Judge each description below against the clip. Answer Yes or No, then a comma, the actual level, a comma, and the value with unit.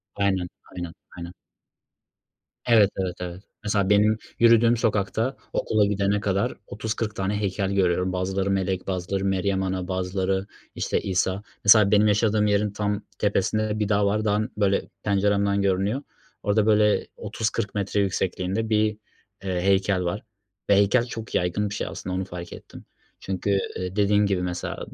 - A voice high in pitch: No, low, 100 Hz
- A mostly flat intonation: Yes, narrow, 1.8 semitones